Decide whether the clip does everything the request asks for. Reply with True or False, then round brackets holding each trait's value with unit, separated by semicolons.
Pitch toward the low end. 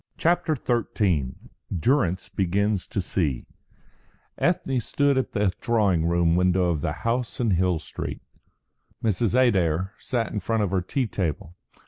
True (100 Hz)